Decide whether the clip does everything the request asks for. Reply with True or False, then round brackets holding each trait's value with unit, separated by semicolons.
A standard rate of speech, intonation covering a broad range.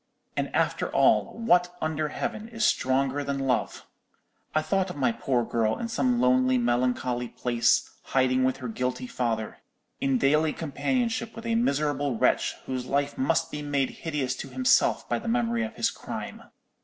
True (170 wpm; 5.8 semitones)